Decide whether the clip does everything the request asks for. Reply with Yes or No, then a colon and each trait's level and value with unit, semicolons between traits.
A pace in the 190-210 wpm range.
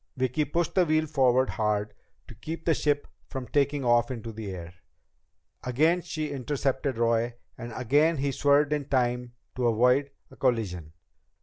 No: average, 160 wpm